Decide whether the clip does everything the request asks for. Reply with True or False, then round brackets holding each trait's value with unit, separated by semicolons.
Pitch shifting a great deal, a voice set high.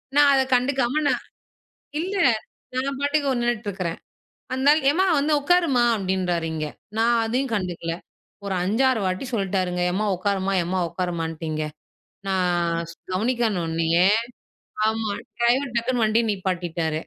True (6.3 semitones; 205 Hz)